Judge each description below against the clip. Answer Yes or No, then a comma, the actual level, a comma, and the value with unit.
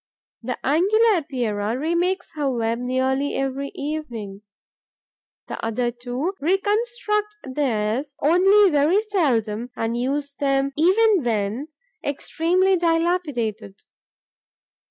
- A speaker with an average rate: No, slow, 95 wpm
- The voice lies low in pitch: No, very high, 280 Hz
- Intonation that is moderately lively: No, wide, 6.7 semitones